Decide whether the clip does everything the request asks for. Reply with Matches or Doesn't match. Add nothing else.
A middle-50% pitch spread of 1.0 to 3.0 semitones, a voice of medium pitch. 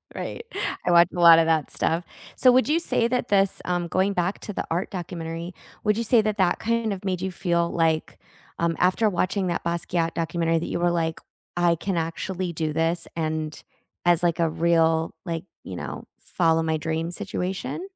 Matches